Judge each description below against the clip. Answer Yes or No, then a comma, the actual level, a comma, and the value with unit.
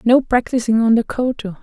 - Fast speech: No, average, 185 wpm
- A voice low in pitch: No, high, 235 Hz